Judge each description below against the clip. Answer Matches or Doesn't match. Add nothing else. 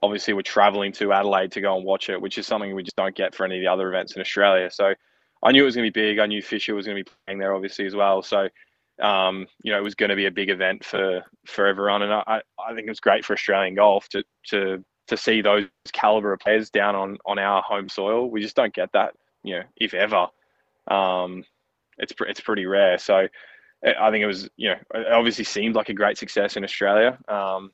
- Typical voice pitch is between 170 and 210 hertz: Doesn't match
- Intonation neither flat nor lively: Doesn't match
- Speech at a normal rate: Doesn't match